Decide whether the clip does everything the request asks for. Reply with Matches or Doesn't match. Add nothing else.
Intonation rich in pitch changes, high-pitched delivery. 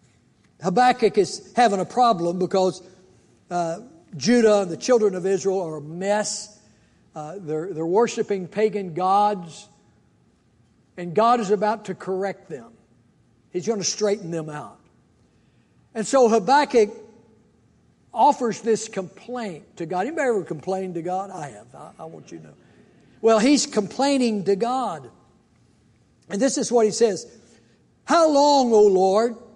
Doesn't match